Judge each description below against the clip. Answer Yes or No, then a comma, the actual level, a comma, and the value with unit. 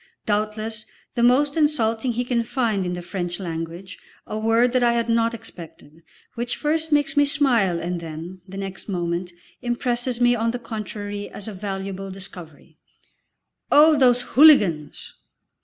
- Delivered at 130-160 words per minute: Yes, average, 155 wpm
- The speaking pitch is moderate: No, high, 220 Hz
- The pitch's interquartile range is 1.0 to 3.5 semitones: No, average, 4.8 semitones